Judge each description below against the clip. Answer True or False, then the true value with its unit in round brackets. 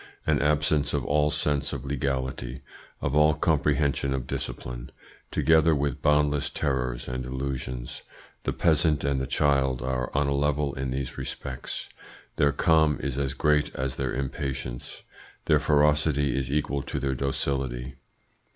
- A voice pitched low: True (70 Hz)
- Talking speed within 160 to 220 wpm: False (145 wpm)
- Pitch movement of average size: False (2.0 semitones)